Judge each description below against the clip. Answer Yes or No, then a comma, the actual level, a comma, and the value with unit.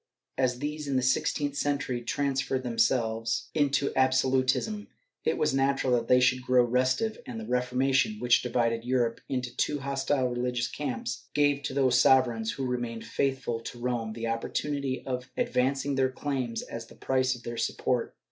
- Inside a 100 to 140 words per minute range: No, average, 165 wpm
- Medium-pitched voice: No, low, 130 Hz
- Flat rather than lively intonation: Yes, narrow, 2.2 semitones